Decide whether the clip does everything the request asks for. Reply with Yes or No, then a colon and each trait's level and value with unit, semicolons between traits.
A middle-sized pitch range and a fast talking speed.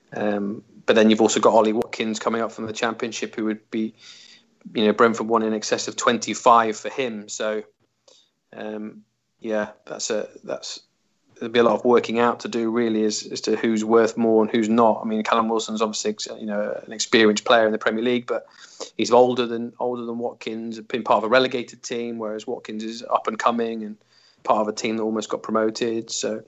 No: narrow, 1.4 semitones; fast, 215 wpm